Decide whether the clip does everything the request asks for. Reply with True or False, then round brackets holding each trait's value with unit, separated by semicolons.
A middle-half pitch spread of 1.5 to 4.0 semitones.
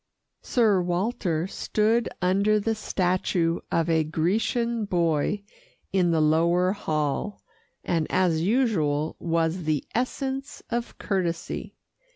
False (4.5 semitones)